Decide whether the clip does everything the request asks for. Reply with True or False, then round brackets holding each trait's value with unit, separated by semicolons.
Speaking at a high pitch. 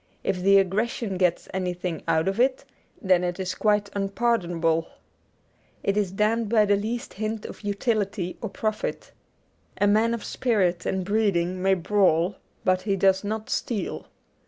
True (195 Hz)